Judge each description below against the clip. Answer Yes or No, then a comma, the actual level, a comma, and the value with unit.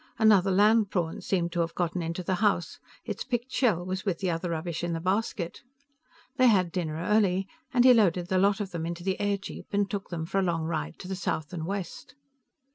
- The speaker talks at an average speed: No, fast, 220 wpm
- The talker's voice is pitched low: No, medium, 185 Hz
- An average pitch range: Yes, average, 3.0 semitones